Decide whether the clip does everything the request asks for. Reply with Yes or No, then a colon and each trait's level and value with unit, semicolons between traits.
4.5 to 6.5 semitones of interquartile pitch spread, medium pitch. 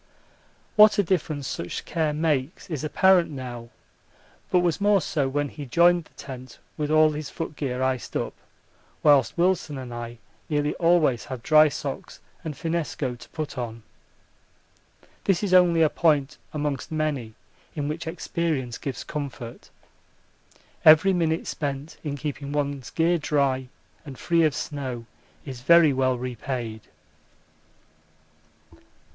No: average, 3.9 semitones; medium, 150 Hz